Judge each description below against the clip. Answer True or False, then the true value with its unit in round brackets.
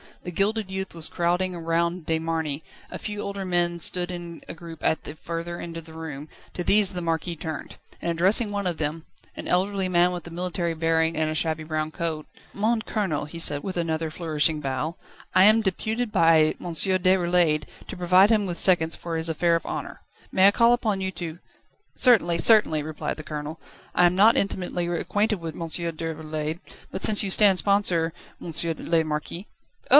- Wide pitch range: False (2.7 semitones)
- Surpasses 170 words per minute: True (200 wpm)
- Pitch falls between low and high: True (170 Hz)